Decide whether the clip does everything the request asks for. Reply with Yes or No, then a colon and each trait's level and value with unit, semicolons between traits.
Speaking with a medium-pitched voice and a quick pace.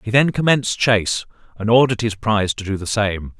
No: low, 110 Hz; fast, 210 wpm